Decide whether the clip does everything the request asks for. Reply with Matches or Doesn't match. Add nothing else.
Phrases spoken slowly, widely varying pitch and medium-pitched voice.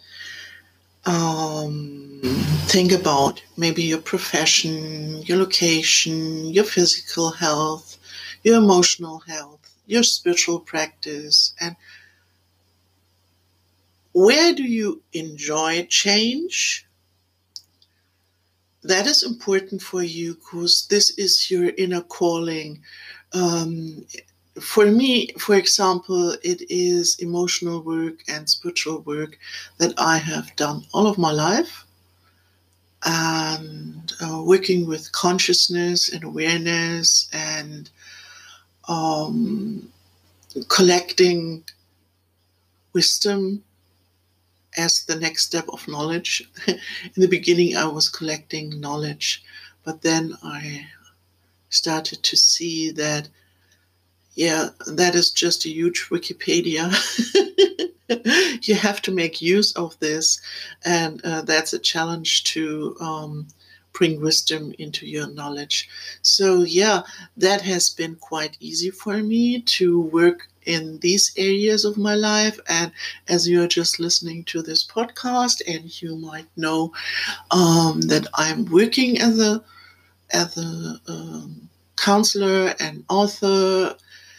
Doesn't match